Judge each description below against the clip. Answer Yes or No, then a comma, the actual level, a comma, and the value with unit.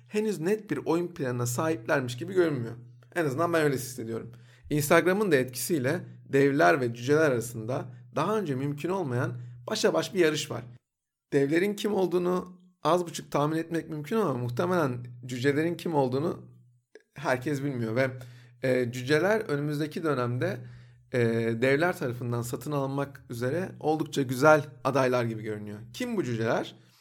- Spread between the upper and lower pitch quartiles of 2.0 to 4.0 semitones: No, average, 4.8 semitones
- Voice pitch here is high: No, medium, 140 Hz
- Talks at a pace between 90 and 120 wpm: No, average, 135 wpm